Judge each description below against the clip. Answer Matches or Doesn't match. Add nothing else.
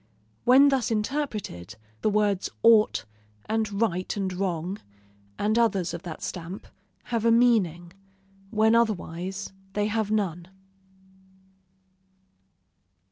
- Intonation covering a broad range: Doesn't match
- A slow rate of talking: Matches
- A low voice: Doesn't match